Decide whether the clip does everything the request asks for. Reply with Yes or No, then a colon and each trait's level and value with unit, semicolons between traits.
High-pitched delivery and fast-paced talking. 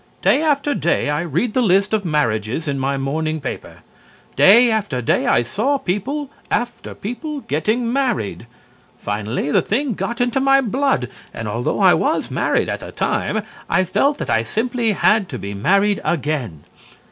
No: high, 195 Hz; average, 170 wpm